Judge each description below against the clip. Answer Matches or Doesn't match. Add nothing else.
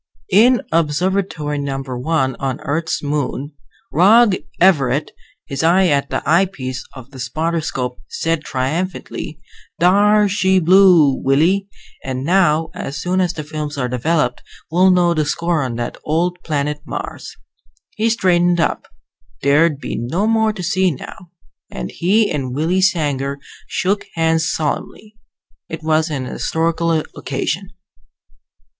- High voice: Doesn't match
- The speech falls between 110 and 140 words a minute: Matches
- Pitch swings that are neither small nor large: Matches